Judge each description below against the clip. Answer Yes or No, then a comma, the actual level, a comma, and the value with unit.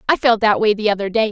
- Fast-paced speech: Yes, fast, 320 wpm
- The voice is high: Yes, high, 215 Hz